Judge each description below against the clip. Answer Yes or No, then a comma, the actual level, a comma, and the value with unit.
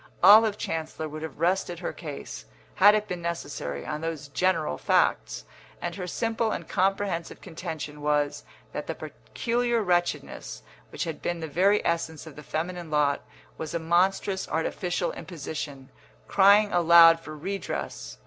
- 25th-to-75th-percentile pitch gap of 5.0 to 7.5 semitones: No, average, 3.6 semitones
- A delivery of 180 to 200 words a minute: No, average, 150 wpm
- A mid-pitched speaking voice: Yes, medium, 170 Hz